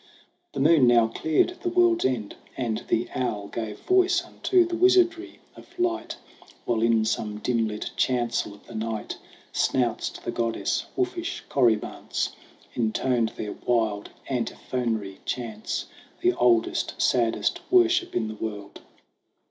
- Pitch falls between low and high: No, low, 120 Hz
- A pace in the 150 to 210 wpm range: No, slow, 135 wpm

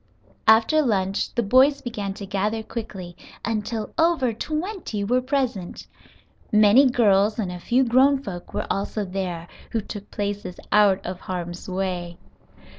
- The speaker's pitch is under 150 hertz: No, high, 210 Hz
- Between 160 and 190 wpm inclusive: No, average, 140 wpm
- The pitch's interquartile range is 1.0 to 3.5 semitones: No, average, 4.4 semitones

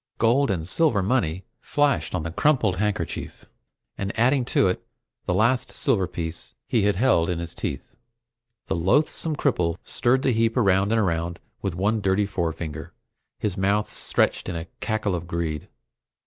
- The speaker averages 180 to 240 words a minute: No, average, 160 wpm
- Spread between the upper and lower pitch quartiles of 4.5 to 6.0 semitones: Yes, average, 5.1 semitones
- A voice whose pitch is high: No, low, 100 Hz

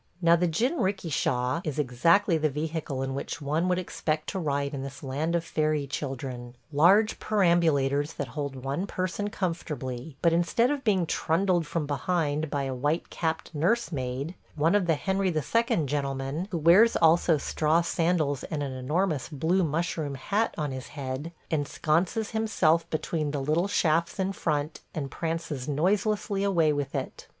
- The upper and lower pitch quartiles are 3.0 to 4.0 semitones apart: Yes, average, 3.7 semitones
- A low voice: No, medium, 160 Hz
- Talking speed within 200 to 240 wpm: No, average, 160 wpm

